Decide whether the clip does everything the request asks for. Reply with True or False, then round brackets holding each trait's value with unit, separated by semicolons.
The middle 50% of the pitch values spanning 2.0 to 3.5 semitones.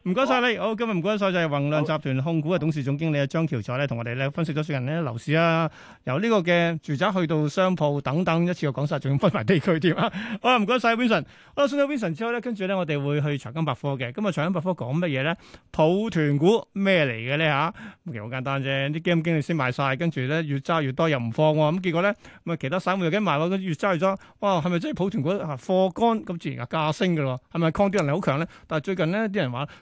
False (4.7 semitones)